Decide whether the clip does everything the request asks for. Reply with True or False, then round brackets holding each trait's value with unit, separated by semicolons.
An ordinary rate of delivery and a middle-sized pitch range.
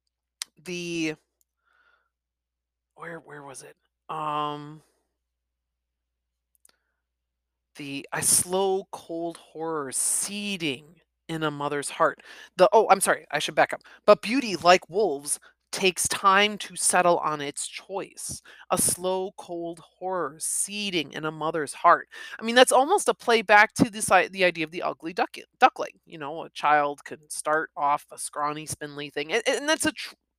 True (150 wpm; 4.9 semitones)